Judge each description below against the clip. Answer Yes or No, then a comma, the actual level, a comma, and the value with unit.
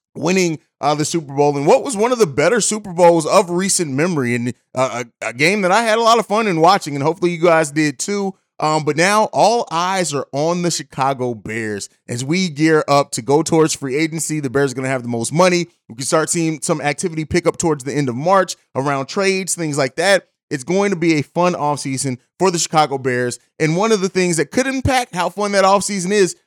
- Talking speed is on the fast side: Yes, fast, 245 wpm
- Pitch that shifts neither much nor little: Yes, average, 4.7 semitones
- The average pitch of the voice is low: No, medium, 160 Hz